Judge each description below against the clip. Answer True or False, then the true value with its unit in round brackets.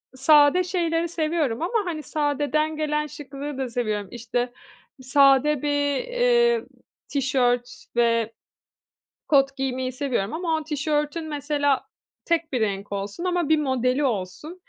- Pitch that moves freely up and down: False (3.8 semitones)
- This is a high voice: True (290 Hz)